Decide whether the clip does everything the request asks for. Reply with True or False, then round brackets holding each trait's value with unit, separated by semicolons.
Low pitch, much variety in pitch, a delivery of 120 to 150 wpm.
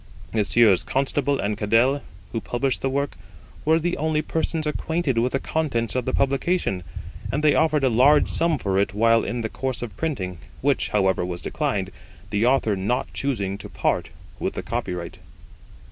False (125 Hz; 5.8 semitones; 175 wpm)